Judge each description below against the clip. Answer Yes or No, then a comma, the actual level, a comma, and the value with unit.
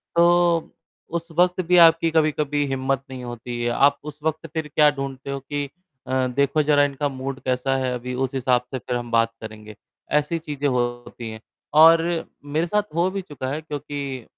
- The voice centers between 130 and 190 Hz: Yes, medium, 140 Hz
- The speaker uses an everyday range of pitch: Yes, average, 3.8 semitones